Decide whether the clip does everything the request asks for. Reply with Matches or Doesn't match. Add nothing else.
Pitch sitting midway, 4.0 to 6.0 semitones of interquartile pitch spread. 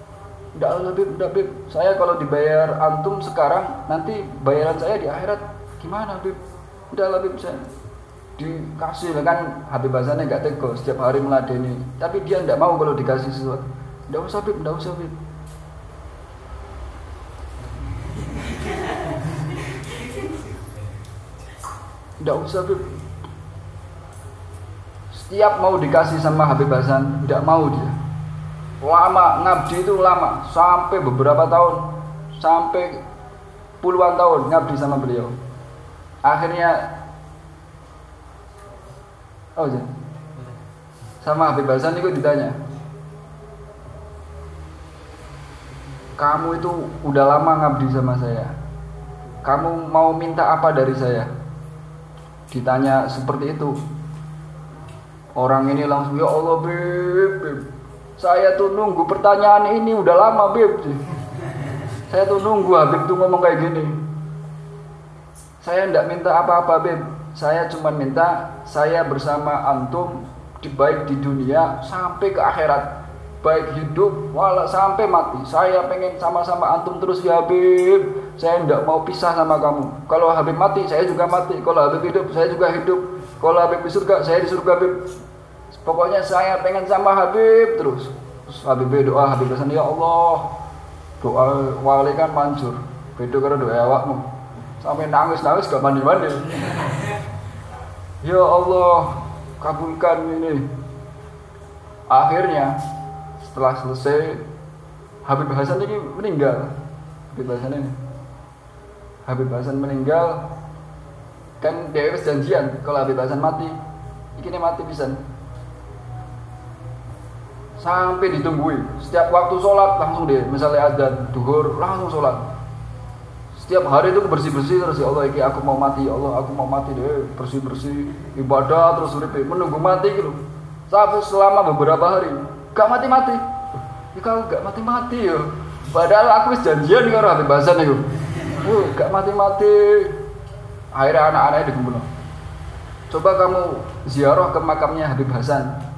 Matches